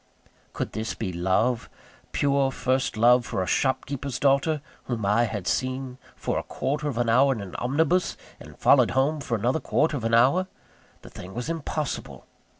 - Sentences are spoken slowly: No, average, 175 wpm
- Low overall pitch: Yes, low, 130 Hz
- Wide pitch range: No, average, 3.5 semitones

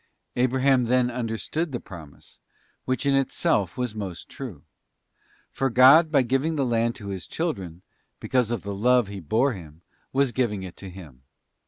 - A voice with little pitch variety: No, average, 5.3 semitones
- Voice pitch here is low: Yes, low, 120 Hz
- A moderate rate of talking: Yes, average, 170 wpm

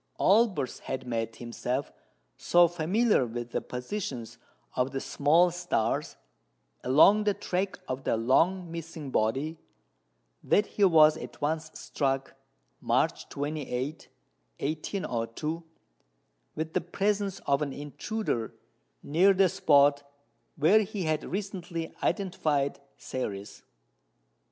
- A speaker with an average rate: No, slow, 110 wpm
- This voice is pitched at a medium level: Yes, medium, 155 Hz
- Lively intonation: Yes, wide, 5.7 semitones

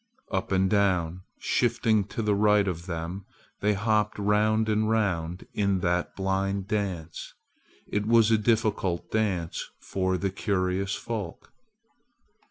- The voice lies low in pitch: Yes, low, 100 Hz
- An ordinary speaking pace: No, slow, 130 wpm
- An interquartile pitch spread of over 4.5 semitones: No, narrow, 2.5 semitones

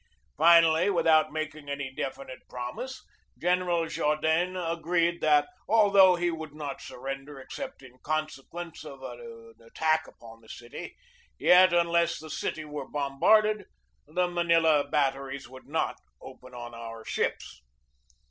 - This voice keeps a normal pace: No, slow, 130 wpm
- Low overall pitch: No, medium, 155 Hz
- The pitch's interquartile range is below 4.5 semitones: Yes, average, 4.1 semitones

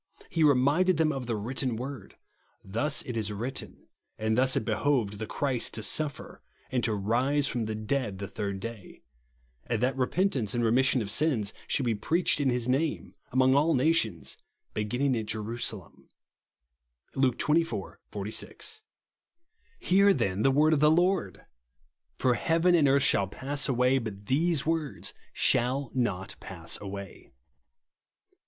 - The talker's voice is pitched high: No, low, 125 Hz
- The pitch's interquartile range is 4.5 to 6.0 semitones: Yes, average, 4.9 semitones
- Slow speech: No, average, 150 wpm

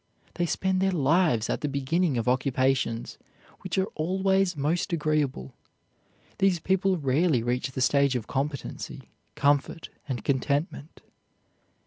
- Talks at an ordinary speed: No, slow, 125 wpm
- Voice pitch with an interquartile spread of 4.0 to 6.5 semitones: Yes, average, 5.1 semitones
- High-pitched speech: No, medium, 145 Hz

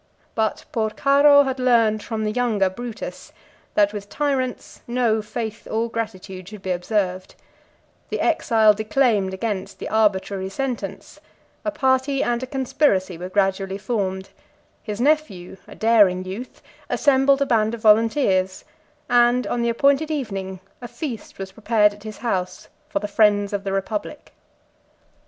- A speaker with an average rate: Yes, average, 145 wpm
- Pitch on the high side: Yes, high, 220 Hz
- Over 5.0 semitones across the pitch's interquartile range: No, average, 4.3 semitones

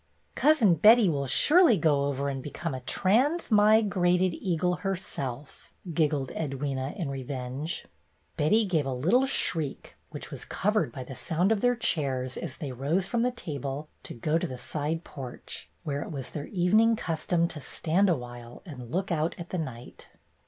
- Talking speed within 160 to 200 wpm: Yes, average, 180 wpm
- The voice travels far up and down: Yes, wide, 6.0 semitones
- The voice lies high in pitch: No, medium, 160 Hz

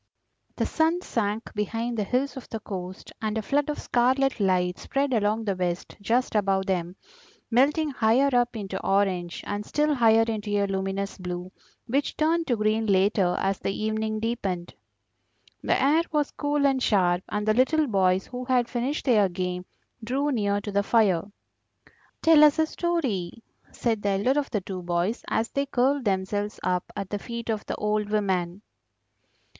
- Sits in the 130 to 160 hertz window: No, high, 215 Hz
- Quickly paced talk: No, average, 175 wpm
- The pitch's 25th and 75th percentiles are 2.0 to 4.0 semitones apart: No, average, 4.8 semitones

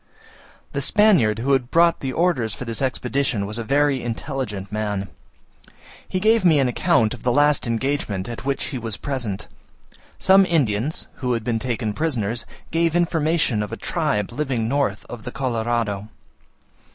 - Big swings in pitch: No, average, 4.8 semitones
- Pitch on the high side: No, low, 125 Hz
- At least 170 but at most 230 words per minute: No, average, 160 wpm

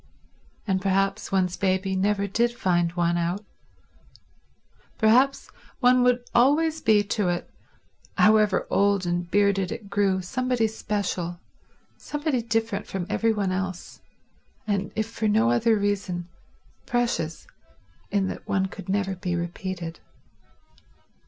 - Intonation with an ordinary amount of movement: Yes, average, 3.2 semitones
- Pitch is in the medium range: No, high, 200 Hz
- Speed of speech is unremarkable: No, slow, 125 wpm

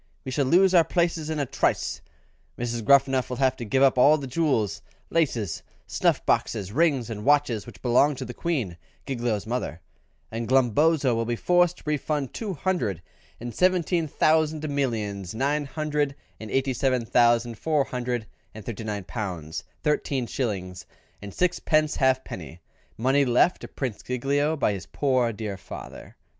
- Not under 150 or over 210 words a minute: Yes, average, 160 wpm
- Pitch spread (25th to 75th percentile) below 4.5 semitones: No, average, 4.9 semitones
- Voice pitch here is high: No, low, 130 Hz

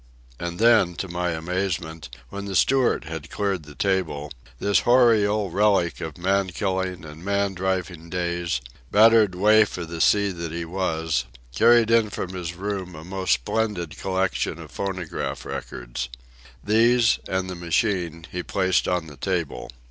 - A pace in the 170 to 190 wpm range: No, average, 155 wpm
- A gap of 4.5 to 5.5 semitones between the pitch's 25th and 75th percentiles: No, average, 3.2 semitones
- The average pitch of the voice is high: No, very low, 95 Hz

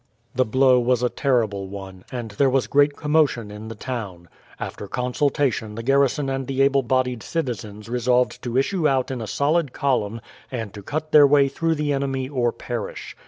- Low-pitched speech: Yes, low, 125 Hz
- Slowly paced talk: No, average, 185 wpm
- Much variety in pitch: No, average, 3.7 semitones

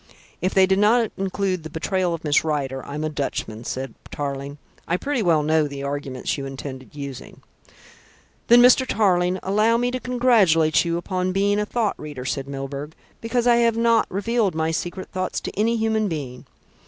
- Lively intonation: Yes, wide, 7.0 semitones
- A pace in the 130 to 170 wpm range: No, average, 180 wpm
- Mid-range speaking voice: Yes, medium, 180 Hz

